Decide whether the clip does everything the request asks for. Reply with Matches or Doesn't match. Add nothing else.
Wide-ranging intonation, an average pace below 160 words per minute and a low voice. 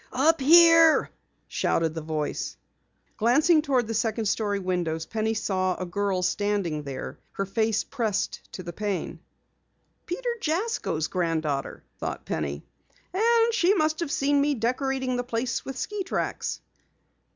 Doesn't match